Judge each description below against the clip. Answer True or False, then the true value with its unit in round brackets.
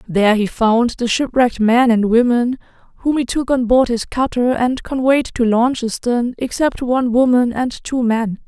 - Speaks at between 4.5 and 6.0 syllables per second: True (4.7 syllables/s)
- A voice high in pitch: True (240 Hz)